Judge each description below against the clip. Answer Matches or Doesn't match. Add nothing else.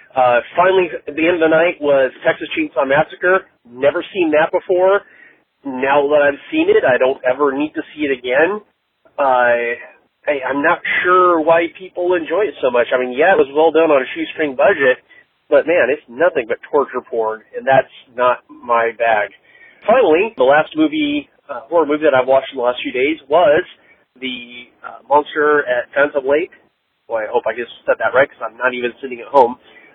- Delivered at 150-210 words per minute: Matches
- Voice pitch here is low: Doesn't match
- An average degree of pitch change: Doesn't match